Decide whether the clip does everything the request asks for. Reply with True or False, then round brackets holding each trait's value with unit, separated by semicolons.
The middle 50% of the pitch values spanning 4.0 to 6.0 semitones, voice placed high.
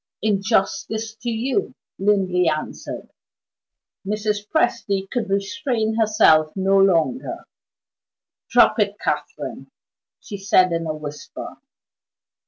False (2.8 semitones; 200 Hz)